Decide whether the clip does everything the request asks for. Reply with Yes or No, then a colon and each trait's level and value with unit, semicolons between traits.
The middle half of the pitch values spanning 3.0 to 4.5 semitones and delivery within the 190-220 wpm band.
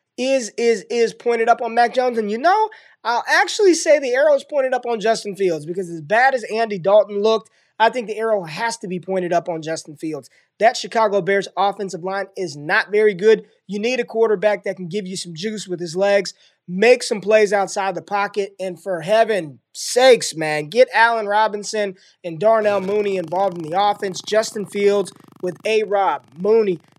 Yes: average, 3.3 semitones; average, 200 wpm